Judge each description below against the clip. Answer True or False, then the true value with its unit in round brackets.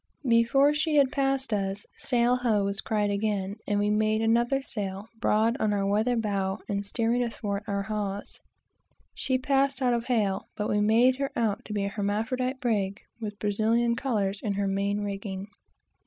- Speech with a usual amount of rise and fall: True (3.2 semitones)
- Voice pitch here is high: True (215 Hz)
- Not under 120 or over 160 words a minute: False (175 wpm)